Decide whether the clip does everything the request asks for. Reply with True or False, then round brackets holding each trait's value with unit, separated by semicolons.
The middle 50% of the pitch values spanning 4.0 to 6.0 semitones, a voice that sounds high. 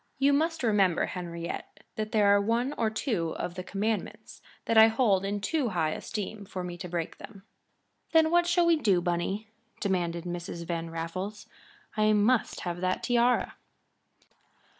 True (4.5 semitones; 205 Hz)